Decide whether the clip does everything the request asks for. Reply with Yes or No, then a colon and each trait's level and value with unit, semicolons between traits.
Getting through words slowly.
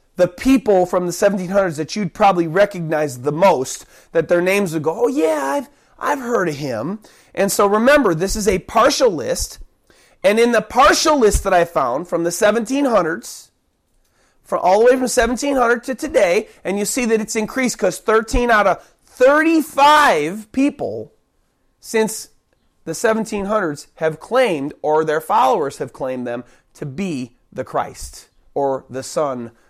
No: average, 165 wpm